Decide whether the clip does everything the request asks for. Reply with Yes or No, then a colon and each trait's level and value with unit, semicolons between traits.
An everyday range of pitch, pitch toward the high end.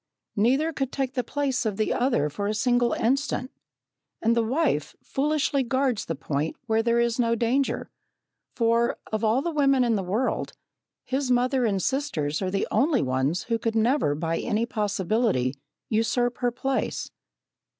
Yes: average, 4.0 semitones; high, 235 Hz